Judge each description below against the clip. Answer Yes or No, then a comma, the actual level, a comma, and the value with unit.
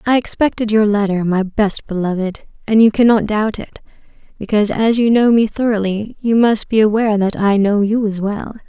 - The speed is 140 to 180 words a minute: No, average, 195 wpm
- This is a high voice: Yes, high, 215 Hz